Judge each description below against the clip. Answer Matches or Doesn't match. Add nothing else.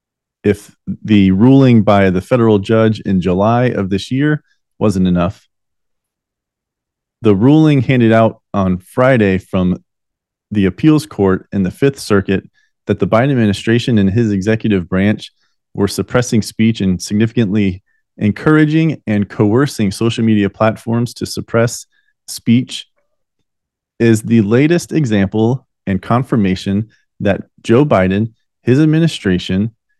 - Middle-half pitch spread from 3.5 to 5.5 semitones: Matches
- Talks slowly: Matches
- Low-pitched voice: Matches